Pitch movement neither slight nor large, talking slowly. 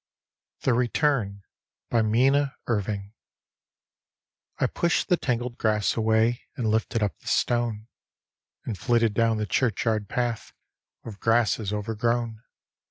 No: narrow, 2.1 semitones; slow, 110 wpm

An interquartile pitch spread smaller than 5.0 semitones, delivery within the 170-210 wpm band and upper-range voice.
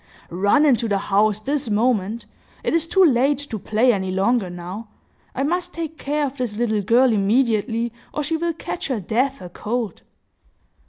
No: average, 5.3 semitones; average, 175 wpm; high, 235 Hz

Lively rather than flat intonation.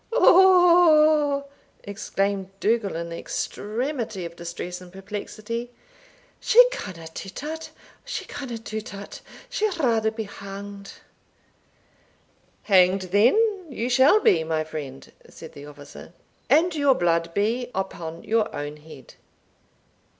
Yes: wide, 7.4 semitones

